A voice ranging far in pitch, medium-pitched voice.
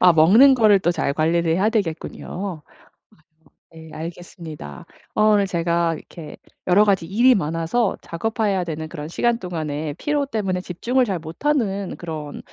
No: average, 4.7 semitones; medium, 180 Hz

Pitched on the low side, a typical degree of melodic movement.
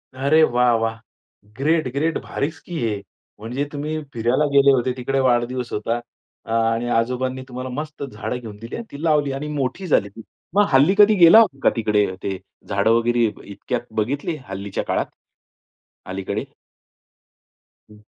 Yes: low, 125 Hz; average, 4.1 semitones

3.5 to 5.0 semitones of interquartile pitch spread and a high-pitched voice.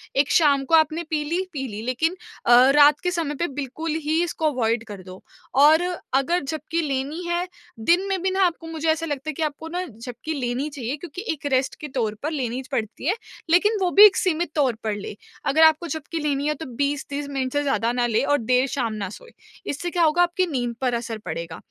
Yes: average, 4.5 semitones; very high, 290 Hz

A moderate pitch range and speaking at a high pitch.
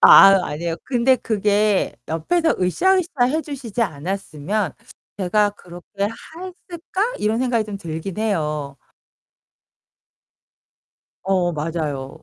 No: wide, 7.3 semitones; high, 205 Hz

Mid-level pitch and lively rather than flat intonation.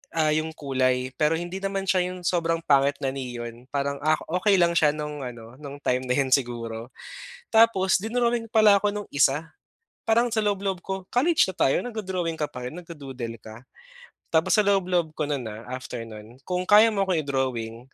Yes: medium, 155 Hz; wide, 6.8 semitones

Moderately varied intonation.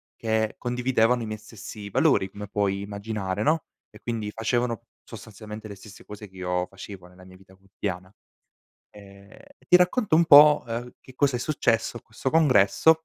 Yes: average, 3.8 semitones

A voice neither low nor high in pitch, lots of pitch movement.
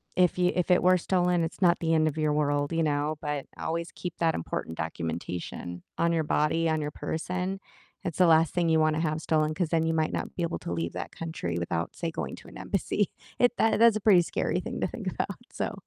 No: medium, 160 Hz; average, 2.8 semitones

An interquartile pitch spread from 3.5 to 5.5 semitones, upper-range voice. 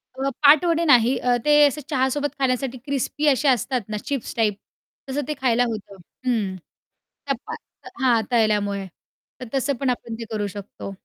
Yes: average, 4.1 semitones; very high, 255 Hz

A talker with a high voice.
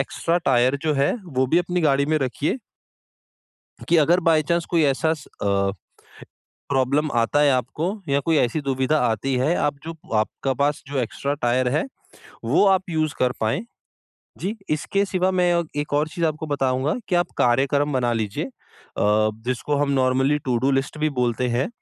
No: medium, 145 Hz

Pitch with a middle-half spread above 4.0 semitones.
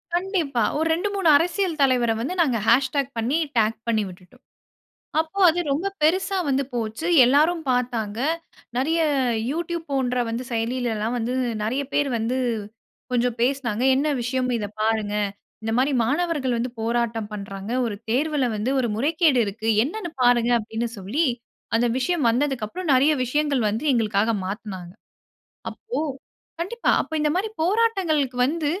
Yes: wide, 5.6 semitones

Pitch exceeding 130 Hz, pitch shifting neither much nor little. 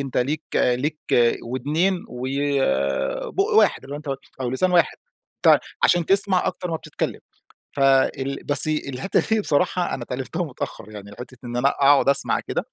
Yes: medium, 140 Hz; average, 4.1 semitones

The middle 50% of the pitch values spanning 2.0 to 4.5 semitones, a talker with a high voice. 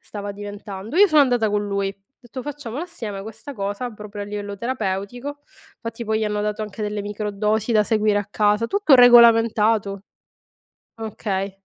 Yes: narrow, 2.5 semitones; high, 215 Hz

